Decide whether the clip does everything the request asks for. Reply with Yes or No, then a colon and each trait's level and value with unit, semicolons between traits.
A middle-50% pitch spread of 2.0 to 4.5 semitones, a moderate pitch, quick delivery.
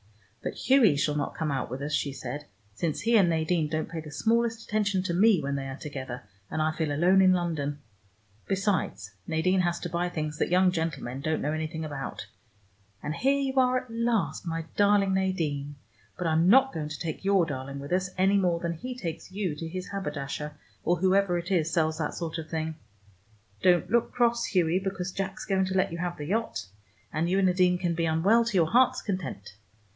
Yes: average, 3.8 semitones; medium, 175 Hz; fast, 210 wpm